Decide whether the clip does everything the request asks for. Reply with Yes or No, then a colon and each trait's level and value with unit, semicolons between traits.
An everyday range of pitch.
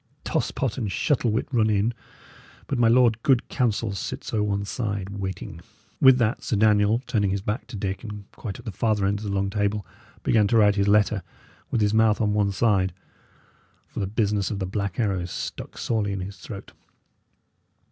No: narrow, 2.1 semitones